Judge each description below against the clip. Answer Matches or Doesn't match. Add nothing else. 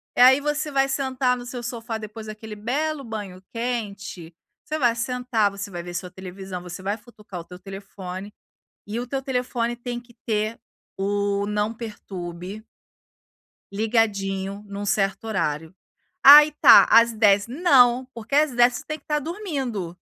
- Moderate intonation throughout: Matches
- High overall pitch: Matches